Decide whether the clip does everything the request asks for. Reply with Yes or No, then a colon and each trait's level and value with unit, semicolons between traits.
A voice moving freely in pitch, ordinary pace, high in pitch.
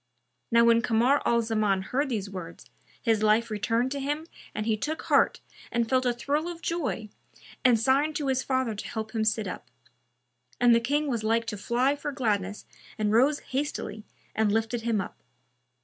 No: average, 3.7 semitones; average, 185 wpm; high, 235 Hz